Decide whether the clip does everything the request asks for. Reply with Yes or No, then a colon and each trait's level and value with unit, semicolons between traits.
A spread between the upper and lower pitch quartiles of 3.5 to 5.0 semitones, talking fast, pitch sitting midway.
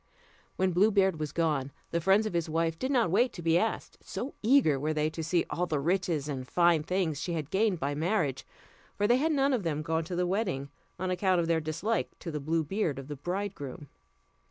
Yes: average, 4.1 semitones; fast, 225 wpm; medium, 170 Hz